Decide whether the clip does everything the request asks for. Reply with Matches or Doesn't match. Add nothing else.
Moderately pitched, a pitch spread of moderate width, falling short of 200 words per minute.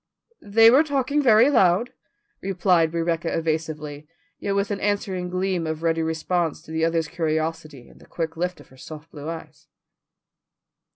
Matches